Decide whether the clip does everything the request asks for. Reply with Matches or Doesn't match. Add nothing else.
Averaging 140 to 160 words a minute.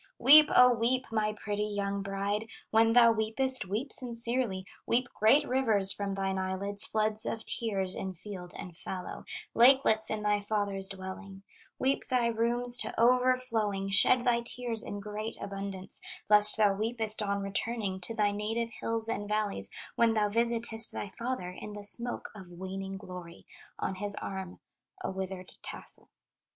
Matches